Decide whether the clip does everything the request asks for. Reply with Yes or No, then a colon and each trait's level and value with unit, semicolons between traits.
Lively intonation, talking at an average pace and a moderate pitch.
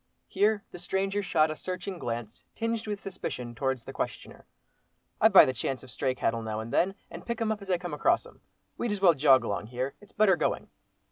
No: wide, 7.8 semitones; fast, 220 wpm; medium, 175 Hz